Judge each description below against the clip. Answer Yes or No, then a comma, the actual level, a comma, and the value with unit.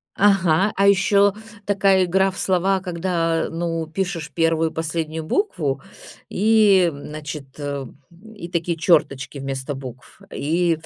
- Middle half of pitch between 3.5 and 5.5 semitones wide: Yes, average, 3.8 semitones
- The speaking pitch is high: No, medium, 170 Hz